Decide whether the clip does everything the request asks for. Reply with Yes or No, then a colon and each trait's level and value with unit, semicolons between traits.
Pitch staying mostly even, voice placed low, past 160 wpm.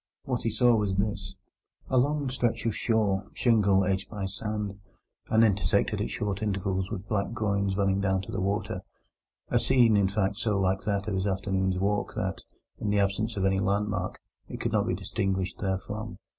Yes: narrow, 1.9 semitones; low, 100 Hz; average, 180 wpm